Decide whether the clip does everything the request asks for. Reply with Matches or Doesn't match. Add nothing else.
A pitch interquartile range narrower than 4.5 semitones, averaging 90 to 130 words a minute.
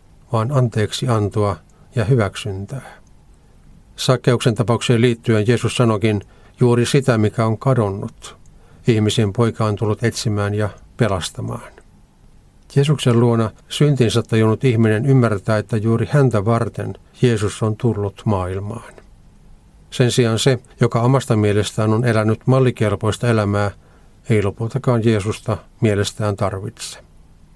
Matches